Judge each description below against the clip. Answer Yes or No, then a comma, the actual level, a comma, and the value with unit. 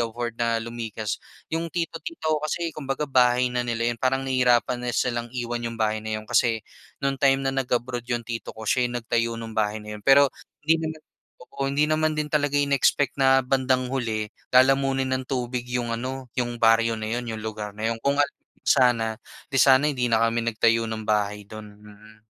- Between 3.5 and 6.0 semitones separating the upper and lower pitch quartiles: No, average, 2.8 semitones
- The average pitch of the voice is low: Yes, low, 120 Hz